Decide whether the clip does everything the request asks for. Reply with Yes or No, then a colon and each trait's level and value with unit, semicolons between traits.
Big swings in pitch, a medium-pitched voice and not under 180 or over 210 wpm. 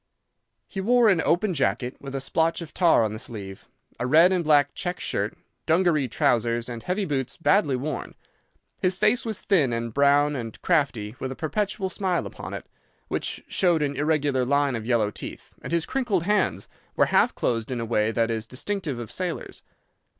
Yes: wide, 7.0 semitones; medium, 145 Hz; average, 185 wpm